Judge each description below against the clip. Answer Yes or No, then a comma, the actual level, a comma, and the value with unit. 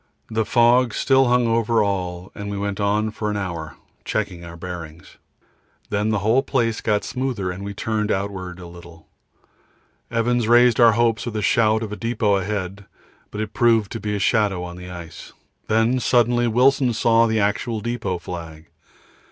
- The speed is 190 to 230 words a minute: No, average, 175 wpm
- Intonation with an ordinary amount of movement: Yes, average, 3.6 semitones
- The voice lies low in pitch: Yes, low, 105 Hz